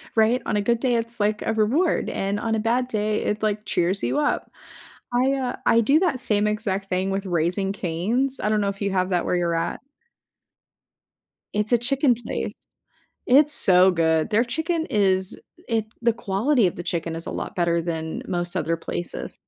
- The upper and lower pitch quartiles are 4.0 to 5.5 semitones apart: Yes, average, 4.6 semitones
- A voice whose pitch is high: Yes, high, 210 Hz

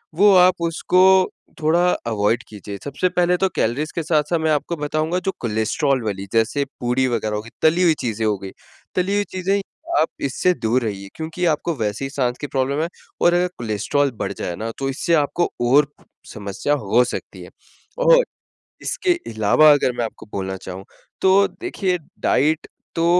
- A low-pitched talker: No, medium, 145 Hz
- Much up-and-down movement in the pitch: Yes, wide, 7.6 semitones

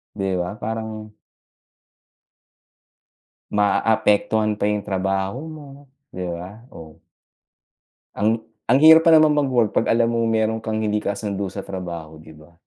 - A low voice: Yes, low, 105 Hz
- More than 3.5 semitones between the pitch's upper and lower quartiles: No, average, 2.9 semitones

